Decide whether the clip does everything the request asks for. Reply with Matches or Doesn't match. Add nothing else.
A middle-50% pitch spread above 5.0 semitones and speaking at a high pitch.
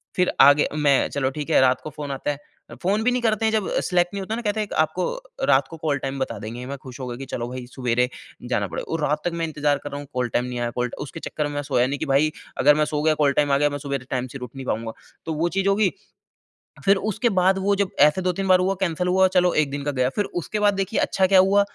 Doesn't match